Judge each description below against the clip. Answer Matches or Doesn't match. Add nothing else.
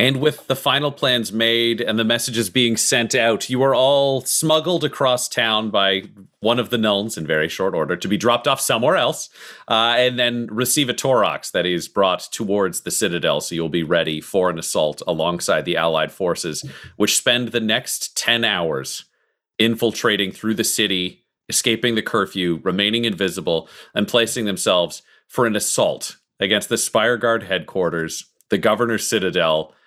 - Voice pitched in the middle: Doesn't match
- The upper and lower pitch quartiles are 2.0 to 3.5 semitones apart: Doesn't match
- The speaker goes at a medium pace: Matches